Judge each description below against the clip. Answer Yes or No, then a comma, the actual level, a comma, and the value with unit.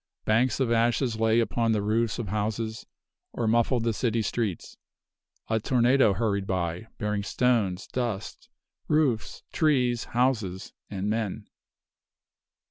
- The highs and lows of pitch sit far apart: No, narrow, 2.5 semitones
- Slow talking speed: Yes, slow, 125 wpm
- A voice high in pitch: No, low, 115 Hz